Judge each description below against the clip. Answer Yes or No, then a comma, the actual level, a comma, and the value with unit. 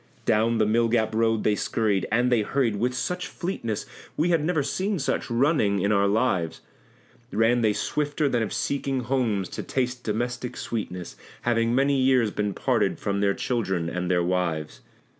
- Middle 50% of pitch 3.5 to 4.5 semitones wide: Yes, average, 4.2 semitones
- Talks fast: No, average, 175 wpm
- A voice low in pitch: Yes, low, 115 Hz